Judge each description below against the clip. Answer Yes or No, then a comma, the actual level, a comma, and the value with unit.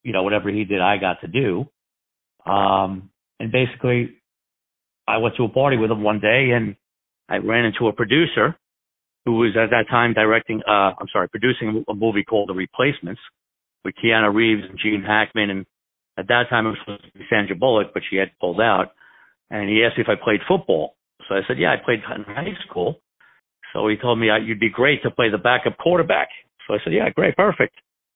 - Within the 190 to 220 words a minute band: Yes, fast, 205 wpm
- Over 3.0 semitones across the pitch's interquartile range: No, narrow, 2.4 semitones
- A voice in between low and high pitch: No, low, 110 Hz